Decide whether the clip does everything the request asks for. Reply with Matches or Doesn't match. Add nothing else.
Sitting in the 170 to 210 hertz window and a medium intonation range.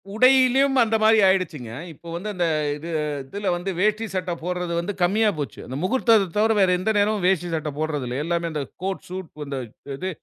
Matches